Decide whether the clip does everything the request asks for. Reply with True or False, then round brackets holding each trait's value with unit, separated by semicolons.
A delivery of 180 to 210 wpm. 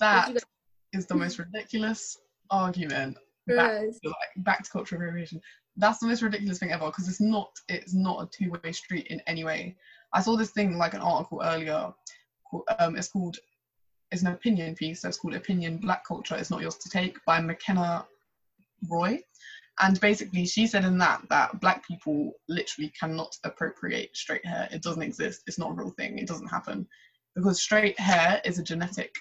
True (185 wpm)